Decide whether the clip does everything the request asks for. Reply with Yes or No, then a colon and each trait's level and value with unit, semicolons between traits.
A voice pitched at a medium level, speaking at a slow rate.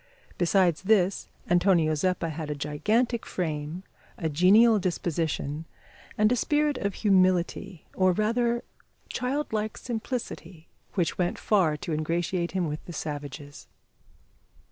Yes: medium, 180 Hz; slow, 120 wpm